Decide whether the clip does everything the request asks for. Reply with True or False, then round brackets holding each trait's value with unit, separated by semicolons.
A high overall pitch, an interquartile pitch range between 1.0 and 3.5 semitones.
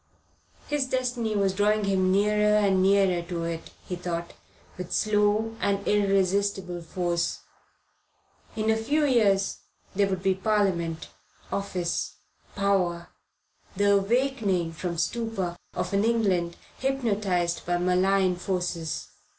True (195 Hz; 2.9 semitones)